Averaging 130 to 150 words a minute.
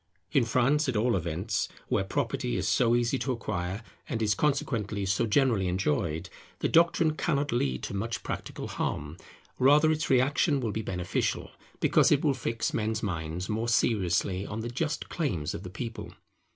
No: average, 170 wpm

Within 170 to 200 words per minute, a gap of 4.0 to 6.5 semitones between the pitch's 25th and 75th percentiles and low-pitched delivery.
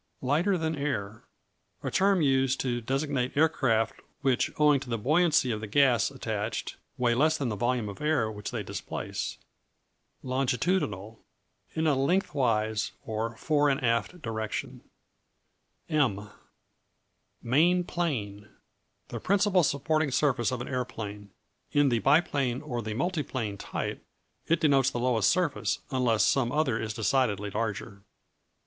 No: slow, 135 wpm; average, 5.1 semitones; low, 130 Hz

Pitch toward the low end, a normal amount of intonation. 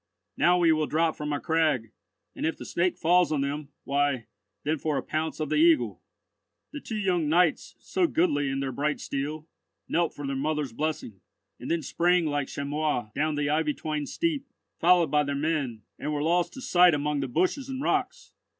No: medium, 155 Hz; average, 3.2 semitones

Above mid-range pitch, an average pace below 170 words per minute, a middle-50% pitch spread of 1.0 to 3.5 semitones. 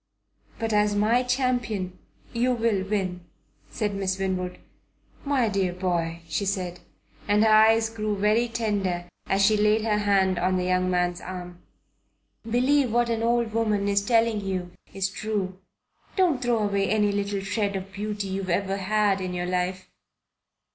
Yes: high, 205 Hz; average, 160 wpm; average, 3.0 semitones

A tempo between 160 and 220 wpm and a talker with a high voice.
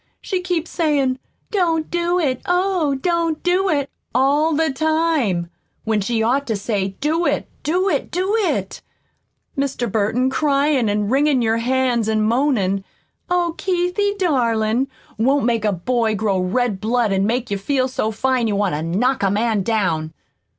Yes: average, 165 wpm; very high, 255 Hz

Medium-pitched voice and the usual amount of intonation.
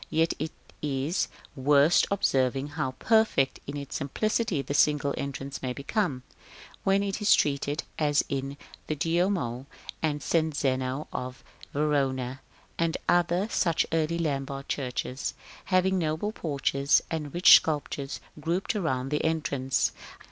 Yes: medium, 145 Hz; average, 3.6 semitones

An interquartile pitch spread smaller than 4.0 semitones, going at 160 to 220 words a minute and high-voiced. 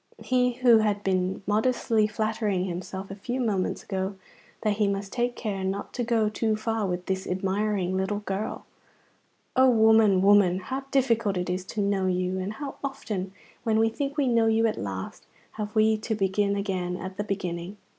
Yes: average, 2.9 semitones; average, 185 wpm; high, 205 Hz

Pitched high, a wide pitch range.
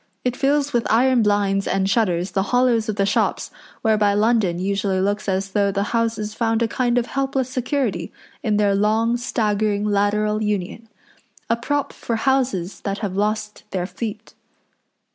No: high, 215 Hz; average, 3.0 semitones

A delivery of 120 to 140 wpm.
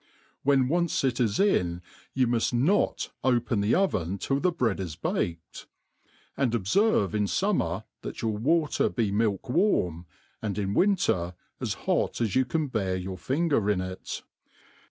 No: average, 160 wpm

